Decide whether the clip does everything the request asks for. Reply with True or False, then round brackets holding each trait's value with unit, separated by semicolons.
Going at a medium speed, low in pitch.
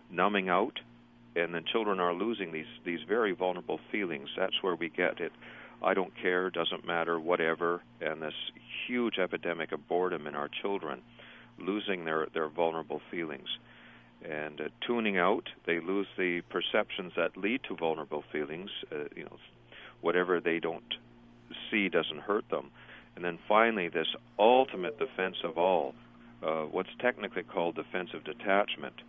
True (155 wpm; 85 Hz)